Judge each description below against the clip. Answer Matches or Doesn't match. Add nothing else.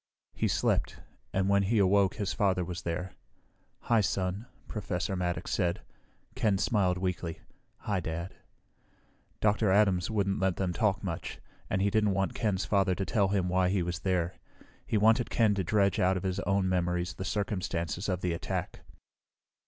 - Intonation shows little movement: Matches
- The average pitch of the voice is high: Doesn't match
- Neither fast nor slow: Matches